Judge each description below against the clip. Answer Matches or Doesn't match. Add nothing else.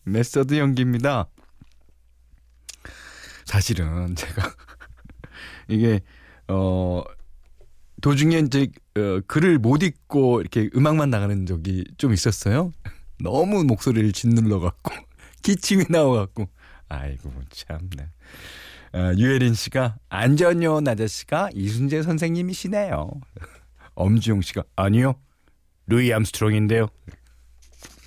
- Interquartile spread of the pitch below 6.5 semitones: Doesn't match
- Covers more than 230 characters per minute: Doesn't match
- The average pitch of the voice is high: Doesn't match